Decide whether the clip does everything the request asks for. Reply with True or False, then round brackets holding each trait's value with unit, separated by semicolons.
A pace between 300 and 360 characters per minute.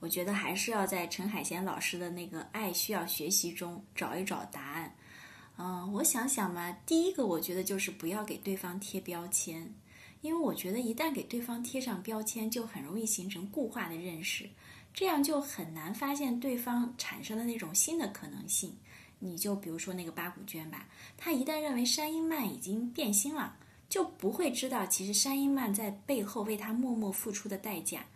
False (290 characters per minute)